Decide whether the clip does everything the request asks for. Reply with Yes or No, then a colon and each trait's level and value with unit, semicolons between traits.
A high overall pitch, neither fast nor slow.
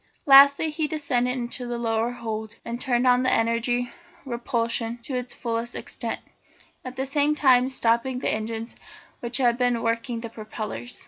Yes: high, 240 Hz; average, 170 wpm